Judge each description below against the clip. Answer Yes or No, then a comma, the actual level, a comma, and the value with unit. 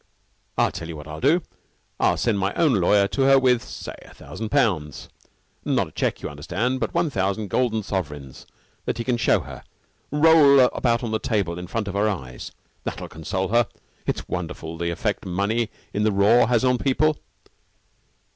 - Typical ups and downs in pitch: No, wide, 5.9 semitones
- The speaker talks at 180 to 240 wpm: Yes, average, 185 wpm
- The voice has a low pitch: Yes, low, 110 Hz